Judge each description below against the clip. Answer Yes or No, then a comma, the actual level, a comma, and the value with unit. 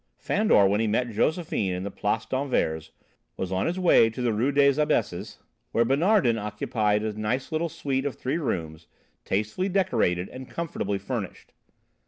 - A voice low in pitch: Yes, low, 115 Hz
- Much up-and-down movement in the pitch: Yes, wide, 5.7 semitones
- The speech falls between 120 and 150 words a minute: No, average, 165 wpm